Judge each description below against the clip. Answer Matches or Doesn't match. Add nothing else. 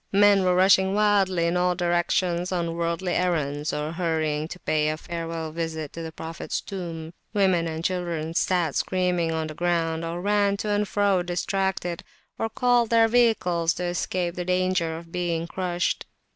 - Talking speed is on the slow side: Doesn't match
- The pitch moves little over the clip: Matches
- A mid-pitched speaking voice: Matches